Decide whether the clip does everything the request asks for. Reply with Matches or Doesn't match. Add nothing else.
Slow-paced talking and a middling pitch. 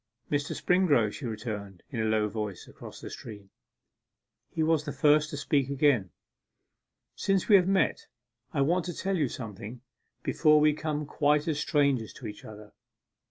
Doesn't match